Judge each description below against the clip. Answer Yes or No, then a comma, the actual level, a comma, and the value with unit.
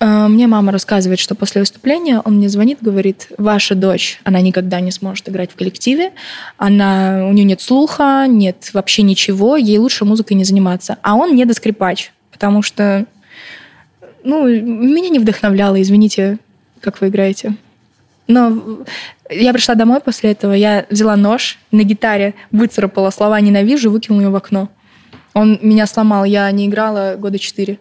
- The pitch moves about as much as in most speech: No, narrow, 2.3 semitones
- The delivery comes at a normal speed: Yes, average, 150 wpm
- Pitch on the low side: No, high, 210 Hz